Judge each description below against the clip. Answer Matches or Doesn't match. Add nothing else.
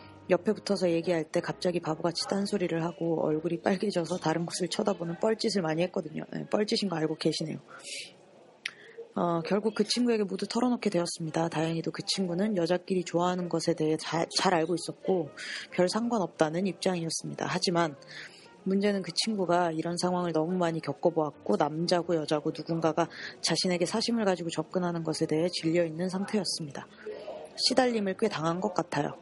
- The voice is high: Doesn't match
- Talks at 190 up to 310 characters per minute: Doesn't match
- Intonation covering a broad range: Doesn't match